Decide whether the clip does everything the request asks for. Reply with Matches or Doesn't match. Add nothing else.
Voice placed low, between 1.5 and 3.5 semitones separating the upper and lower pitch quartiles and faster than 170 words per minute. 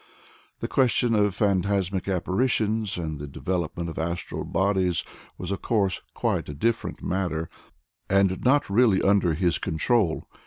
Doesn't match